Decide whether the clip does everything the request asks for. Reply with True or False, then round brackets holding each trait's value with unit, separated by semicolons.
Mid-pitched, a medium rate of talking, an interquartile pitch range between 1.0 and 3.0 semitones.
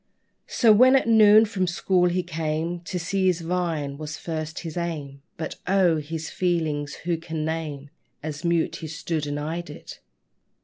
True (165 Hz; 170 wpm; 2.7 semitones)